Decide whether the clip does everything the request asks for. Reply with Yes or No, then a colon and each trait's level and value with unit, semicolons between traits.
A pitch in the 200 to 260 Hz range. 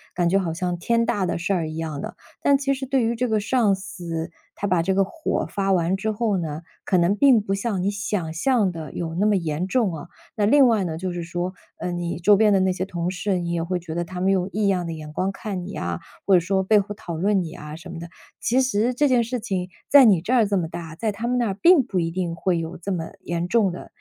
No: high, 190 Hz